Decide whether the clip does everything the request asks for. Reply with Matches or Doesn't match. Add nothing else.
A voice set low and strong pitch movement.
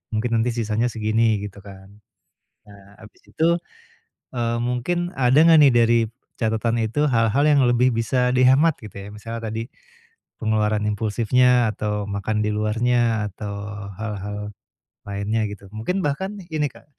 Doesn't match